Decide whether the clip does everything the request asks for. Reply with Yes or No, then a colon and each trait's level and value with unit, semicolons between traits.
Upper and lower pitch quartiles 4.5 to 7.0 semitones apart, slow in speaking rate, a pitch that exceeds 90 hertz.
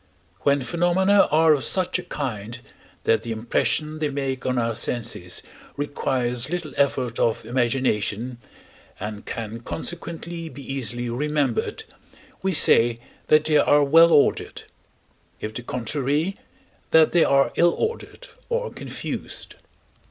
Yes: average, 5.2 semitones; slow, 130 wpm; medium, 140 Hz